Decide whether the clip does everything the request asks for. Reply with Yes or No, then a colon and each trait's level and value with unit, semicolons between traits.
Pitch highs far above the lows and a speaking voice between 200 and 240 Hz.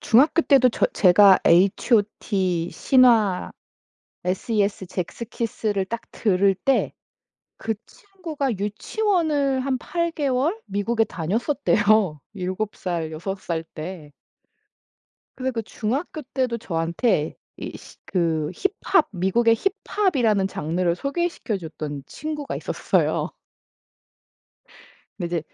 Yes: wide, 6.5 semitones; high, 215 Hz